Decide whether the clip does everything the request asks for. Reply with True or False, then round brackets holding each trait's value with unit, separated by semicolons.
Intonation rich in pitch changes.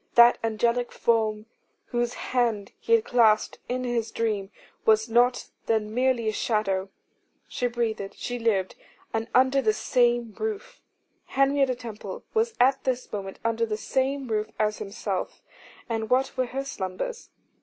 False (2.9 semitones)